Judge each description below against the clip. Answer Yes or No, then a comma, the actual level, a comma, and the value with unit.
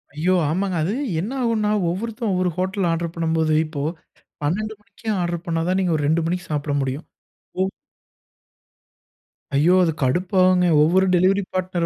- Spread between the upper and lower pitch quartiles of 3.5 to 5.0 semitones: No, average, 2.7 semitones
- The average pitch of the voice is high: No, medium, 180 Hz